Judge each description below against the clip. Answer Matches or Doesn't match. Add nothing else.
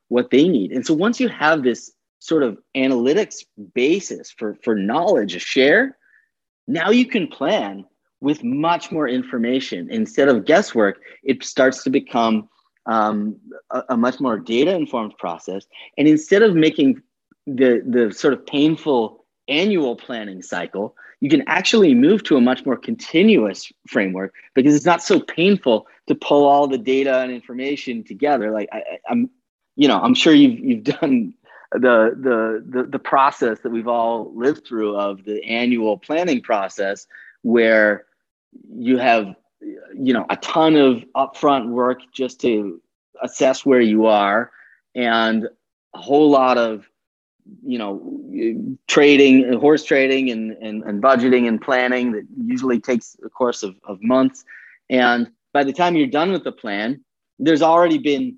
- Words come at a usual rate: Matches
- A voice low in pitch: Matches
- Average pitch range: Doesn't match